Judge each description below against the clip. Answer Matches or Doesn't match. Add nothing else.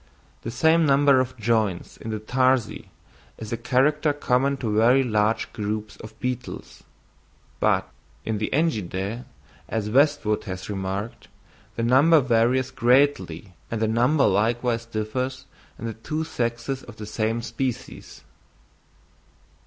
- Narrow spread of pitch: Doesn't match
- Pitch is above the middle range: Doesn't match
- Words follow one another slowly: Matches